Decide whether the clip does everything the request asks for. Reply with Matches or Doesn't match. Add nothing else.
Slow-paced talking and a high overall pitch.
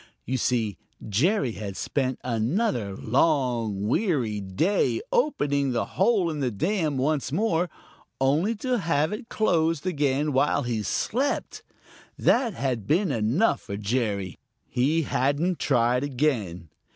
Doesn't match